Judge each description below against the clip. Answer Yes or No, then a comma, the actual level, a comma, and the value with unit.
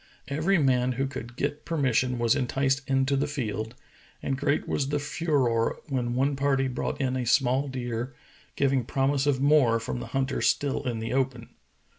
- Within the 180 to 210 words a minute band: Yes, average, 185 wpm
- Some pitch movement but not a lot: No, narrow, 2.3 semitones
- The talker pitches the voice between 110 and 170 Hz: Yes, low, 135 Hz